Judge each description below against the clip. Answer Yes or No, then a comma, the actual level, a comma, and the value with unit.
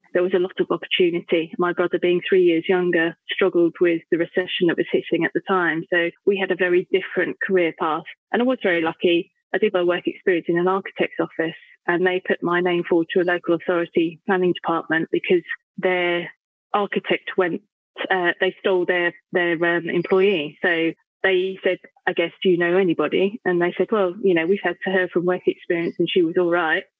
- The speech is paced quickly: Yes, fast, 210 wpm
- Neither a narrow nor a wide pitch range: No, narrow, 1.7 semitones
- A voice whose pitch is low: No, medium, 180 Hz